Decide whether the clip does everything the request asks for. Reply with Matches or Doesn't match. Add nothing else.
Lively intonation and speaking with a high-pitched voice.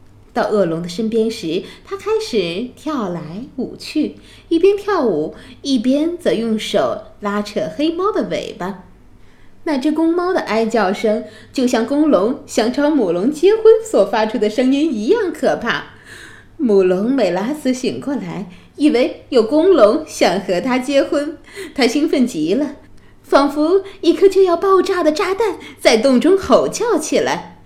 Matches